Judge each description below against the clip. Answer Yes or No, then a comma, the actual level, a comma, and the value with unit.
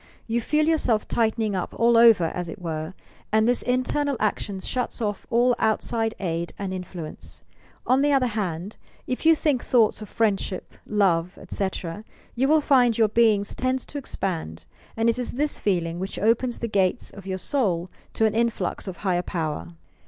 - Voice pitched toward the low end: No, high, 215 Hz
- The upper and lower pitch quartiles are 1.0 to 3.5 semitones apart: No, average, 4.8 semitones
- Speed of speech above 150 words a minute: Yes, average, 175 wpm